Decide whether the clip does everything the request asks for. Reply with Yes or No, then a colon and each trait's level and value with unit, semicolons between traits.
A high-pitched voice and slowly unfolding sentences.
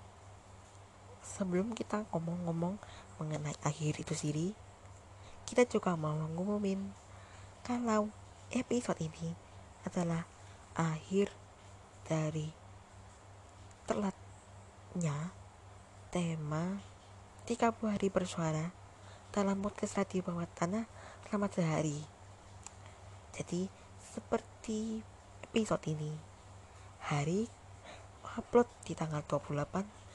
No: medium, 155 Hz; slow, 75 wpm